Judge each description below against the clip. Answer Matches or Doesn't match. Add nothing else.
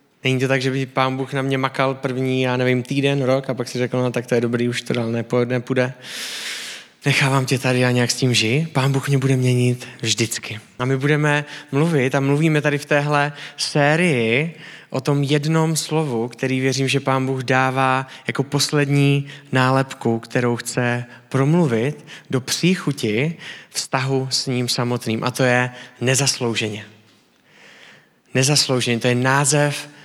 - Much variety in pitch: Doesn't match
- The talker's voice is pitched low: Matches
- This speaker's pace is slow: Doesn't match